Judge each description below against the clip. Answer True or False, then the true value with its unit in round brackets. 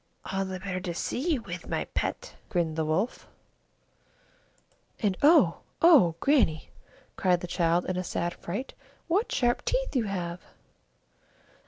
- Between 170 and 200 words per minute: False (150 wpm)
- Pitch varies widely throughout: True (6.6 semitones)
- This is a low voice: False (185 Hz)